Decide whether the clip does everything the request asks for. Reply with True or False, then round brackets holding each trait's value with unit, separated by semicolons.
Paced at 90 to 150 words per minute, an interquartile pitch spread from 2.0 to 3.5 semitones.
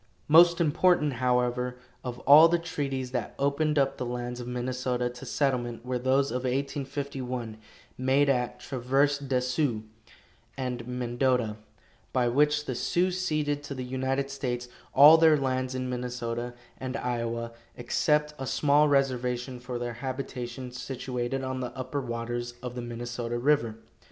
True (145 wpm; 2.4 semitones)